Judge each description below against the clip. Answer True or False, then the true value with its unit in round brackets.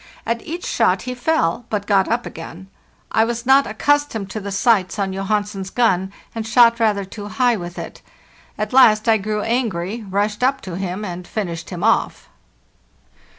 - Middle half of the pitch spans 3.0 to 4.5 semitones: True (3.5 semitones)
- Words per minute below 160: False (175 wpm)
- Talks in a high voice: True (215 Hz)